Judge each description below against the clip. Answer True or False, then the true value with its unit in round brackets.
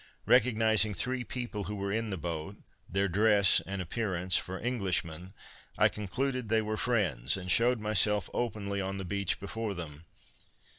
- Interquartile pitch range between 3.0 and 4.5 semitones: True (3.3 semitones)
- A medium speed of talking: True (155 wpm)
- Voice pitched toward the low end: True (100 Hz)